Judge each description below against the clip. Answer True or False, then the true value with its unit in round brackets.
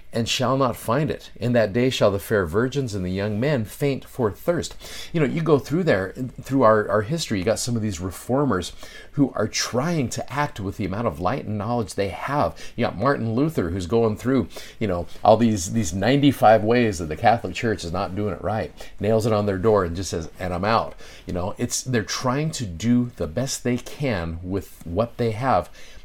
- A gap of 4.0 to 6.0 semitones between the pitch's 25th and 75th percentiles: True (4.3 semitones)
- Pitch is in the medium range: False (115 Hz)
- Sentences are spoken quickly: True (225 wpm)